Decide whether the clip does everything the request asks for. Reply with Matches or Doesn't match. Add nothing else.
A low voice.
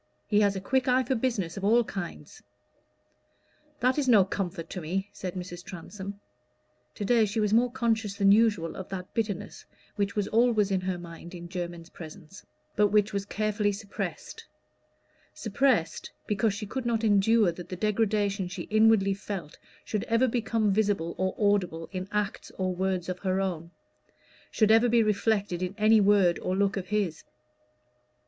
Doesn't match